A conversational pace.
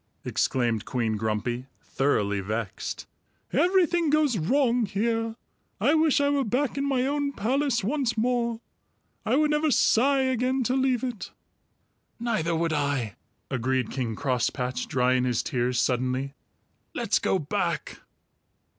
No: slow, 130 wpm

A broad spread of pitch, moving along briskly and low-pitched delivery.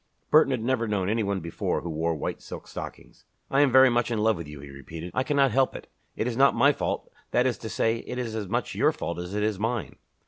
Yes: wide, 6.2 semitones; fast, 265 wpm; low, 110 Hz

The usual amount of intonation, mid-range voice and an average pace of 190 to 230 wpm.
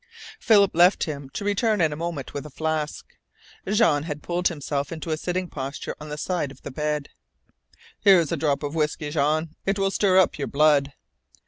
Yes: average, 3.5 semitones; medium, 155 Hz; average, 195 wpm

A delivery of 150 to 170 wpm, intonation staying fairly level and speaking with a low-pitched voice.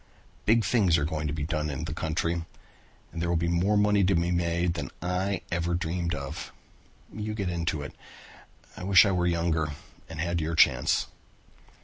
No: average, 190 wpm; narrow, 2.0 semitones; very low, 85 Hz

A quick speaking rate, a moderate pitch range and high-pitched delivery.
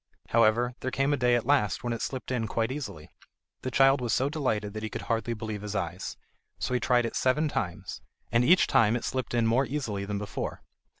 No: fast, 225 wpm; average, 3.3 semitones; low, 120 Hz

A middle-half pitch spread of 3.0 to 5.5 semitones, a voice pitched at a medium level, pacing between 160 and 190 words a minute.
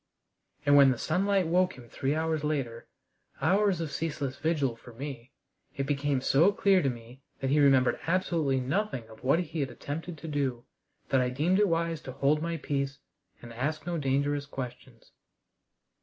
Yes: average, 3.9 semitones; medium, 145 Hz; average, 175 wpm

